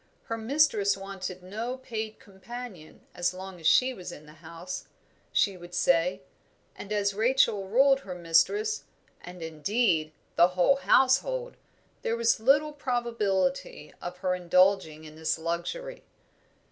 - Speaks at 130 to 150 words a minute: Yes, slow, 135 wpm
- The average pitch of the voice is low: No, high, 195 Hz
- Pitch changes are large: Yes, wide, 5.9 semitones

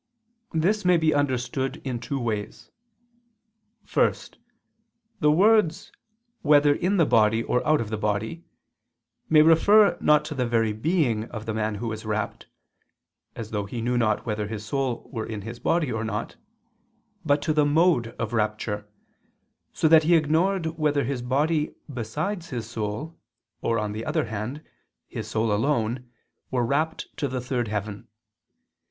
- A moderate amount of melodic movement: No, wide, 5.9 semitones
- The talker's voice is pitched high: No, low, 125 Hz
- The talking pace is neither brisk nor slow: Yes, average, 160 wpm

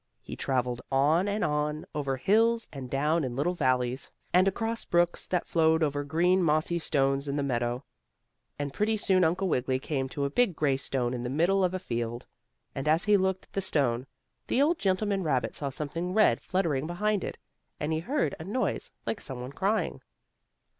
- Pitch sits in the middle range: Yes, medium, 155 Hz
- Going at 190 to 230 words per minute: Yes, average, 195 wpm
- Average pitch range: No, wide, 5.7 semitones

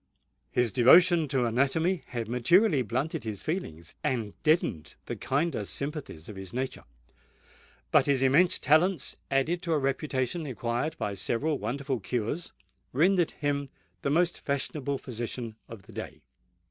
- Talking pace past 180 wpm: No, average, 140 wpm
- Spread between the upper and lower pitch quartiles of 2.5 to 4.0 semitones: No, average, 5.1 semitones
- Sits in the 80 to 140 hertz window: Yes, low, 135 Hz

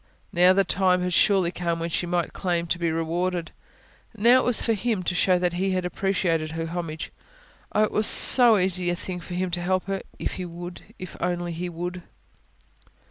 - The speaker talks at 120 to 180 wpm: No, fast, 205 wpm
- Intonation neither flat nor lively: No, narrow, 1.6 semitones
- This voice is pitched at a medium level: Yes, medium, 180 Hz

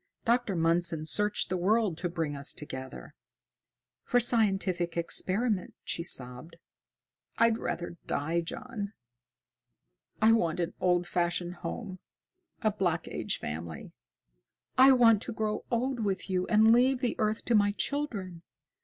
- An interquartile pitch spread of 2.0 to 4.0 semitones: No, average, 4.8 semitones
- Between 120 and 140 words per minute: Yes, slow, 135 wpm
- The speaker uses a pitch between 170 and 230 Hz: Yes, high, 190 Hz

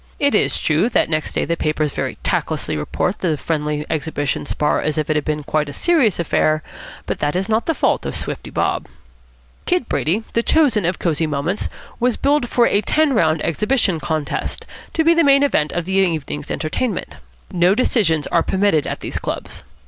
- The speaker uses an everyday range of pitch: No, wide, 7.2 semitones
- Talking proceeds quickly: No, average, 195 wpm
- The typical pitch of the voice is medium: Yes, medium, 170 Hz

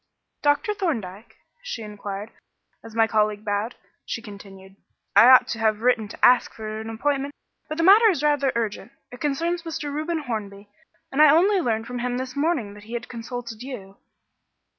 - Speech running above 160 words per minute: Yes, average, 185 wpm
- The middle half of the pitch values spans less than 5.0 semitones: No, average, 5.3 semitones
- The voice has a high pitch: Yes, high, 240 Hz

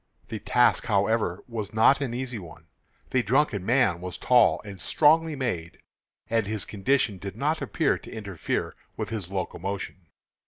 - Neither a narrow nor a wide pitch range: Yes, average, 4.7 semitones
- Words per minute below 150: No, average, 155 wpm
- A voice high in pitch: No, low, 110 Hz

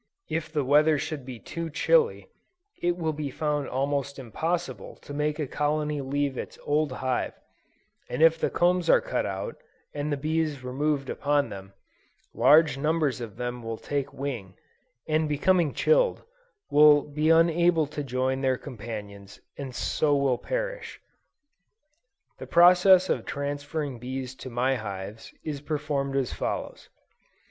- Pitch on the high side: No, medium, 145 Hz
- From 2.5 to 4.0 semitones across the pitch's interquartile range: Yes, average, 3.2 semitones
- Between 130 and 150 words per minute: Yes, average, 145 wpm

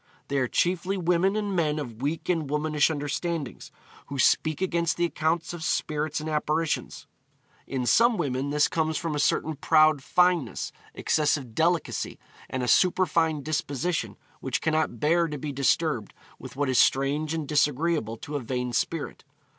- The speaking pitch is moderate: Yes, medium, 155 Hz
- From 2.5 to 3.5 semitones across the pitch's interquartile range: Yes, average, 3.0 semitones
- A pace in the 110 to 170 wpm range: Yes, average, 160 wpm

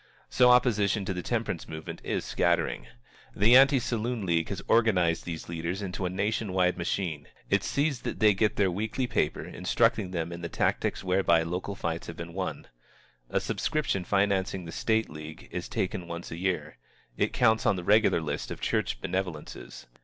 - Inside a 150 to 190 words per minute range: Yes, average, 180 wpm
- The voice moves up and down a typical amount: Yes, average, 4.3 semitones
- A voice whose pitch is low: Yes, very low, 95 Hz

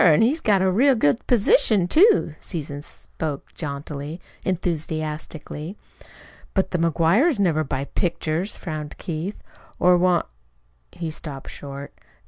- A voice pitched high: No, medium, 165 Hz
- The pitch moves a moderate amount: Yes, average, 4.3 semitones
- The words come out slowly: Yes, slow, 125 wpm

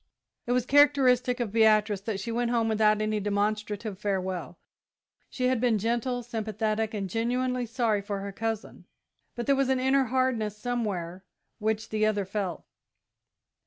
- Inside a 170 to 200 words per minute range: No, average, 155 wpm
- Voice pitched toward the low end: No, high, 220 Hz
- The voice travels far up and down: No, average, 2.8 semitones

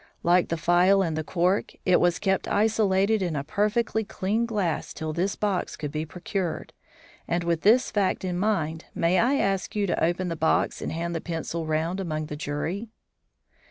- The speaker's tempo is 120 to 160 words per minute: No, average, 190 wpm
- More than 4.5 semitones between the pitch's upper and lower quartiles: No, average, 3.5 semitones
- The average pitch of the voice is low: No, medium, 180 Hz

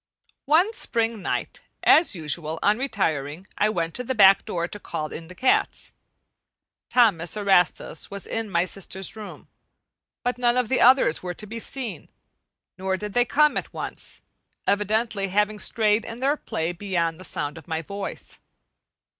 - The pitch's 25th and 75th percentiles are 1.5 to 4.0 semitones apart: No, average, 5.0 semitones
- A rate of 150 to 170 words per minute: Yes, average, 165 wpm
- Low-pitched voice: No, high, 205 Hz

